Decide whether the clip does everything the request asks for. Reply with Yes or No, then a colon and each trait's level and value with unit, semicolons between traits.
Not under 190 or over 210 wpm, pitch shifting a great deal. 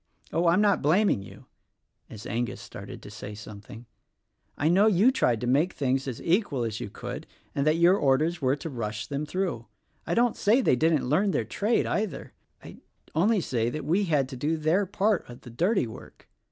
Yes: average, 195 wpm; wide, 7.6 semitones